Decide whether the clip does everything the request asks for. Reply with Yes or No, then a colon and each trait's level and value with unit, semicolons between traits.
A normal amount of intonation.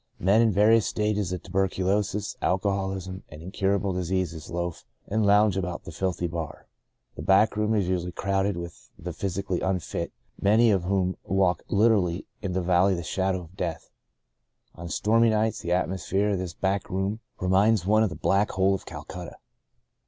No: narrow, 2.2 semitones